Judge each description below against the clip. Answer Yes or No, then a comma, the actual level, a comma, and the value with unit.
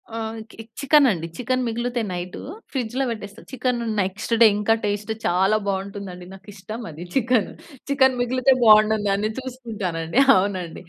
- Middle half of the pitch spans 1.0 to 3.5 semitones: No, average, 4.1 semitones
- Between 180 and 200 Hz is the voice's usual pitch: No, high, 215 Hz